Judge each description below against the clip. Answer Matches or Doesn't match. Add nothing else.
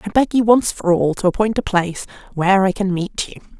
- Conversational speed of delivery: Doesn't match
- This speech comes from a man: Doesn't match